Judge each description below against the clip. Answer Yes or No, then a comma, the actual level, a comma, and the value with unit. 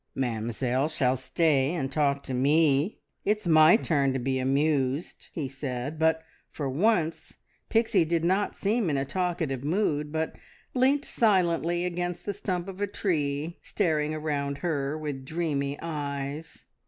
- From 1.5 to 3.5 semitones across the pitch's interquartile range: No, average, 3.9 semitones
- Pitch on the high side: No, medium, 155 Hz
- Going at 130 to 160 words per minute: Yes, average, 145 wpm